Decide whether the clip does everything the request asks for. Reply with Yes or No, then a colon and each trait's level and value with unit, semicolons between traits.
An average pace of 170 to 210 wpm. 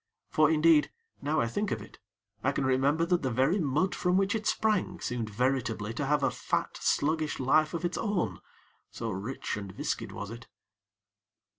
Yes: average, 180 wpm